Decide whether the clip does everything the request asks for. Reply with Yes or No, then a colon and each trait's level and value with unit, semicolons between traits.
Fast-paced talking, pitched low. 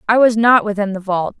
No: fast, 255 wpm; high, 210 Hz